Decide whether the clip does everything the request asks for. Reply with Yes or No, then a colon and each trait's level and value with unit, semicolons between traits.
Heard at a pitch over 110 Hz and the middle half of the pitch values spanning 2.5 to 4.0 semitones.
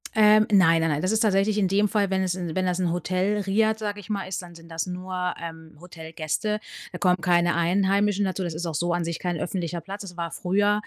Yes: medium, 185 Hz; average, 2.9 semitones